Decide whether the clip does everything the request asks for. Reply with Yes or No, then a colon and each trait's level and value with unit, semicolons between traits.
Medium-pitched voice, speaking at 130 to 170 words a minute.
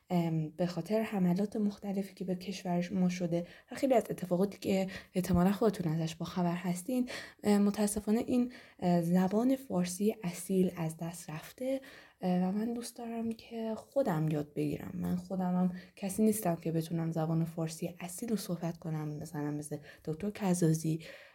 Yes: medium, 180 Hz; average, 150 wpm